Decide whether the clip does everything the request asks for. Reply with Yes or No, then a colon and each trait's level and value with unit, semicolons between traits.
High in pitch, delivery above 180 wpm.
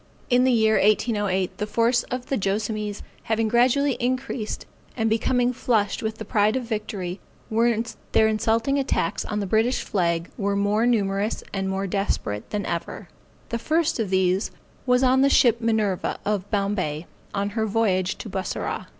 No: high, 215 Hz; average, 160 wpm